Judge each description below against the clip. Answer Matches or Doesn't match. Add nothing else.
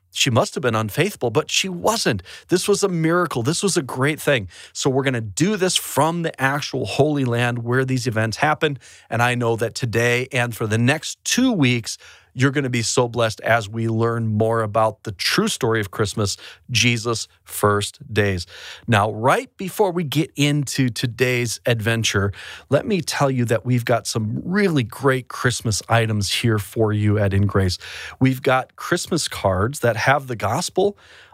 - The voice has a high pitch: Doesn't match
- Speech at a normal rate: Matches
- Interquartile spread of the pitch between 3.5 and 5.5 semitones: Matches